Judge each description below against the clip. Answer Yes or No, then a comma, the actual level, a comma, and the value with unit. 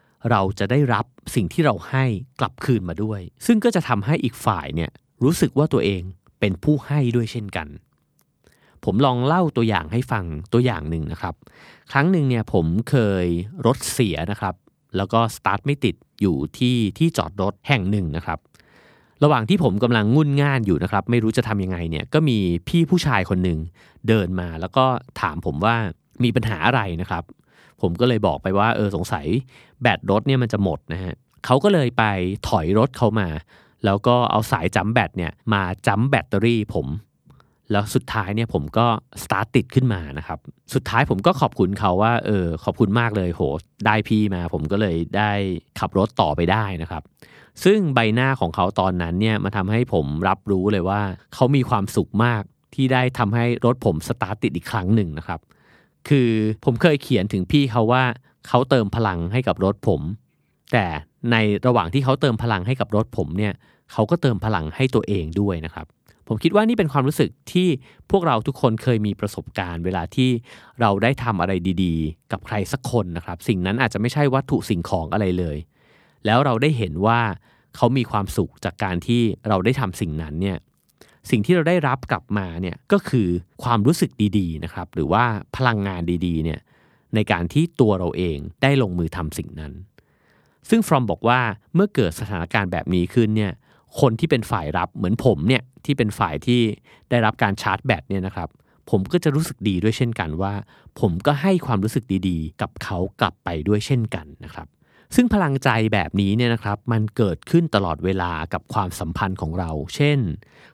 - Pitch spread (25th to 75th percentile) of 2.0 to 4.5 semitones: No, average, 5.2 semitones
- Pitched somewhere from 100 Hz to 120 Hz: Yes, low, 110 Hz